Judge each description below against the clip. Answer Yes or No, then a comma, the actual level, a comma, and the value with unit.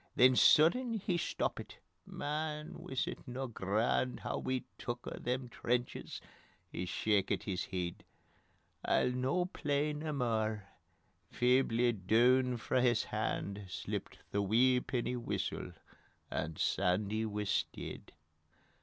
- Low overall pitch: Yes, low, 125 Hz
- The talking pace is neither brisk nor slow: No, slow, 125 wpm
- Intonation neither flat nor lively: Yes, average, 3.9 semitones